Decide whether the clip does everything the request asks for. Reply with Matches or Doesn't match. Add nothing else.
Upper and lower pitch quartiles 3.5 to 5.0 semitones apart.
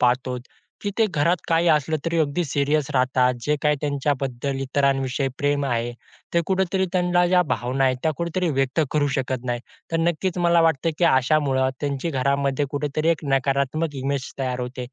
Matches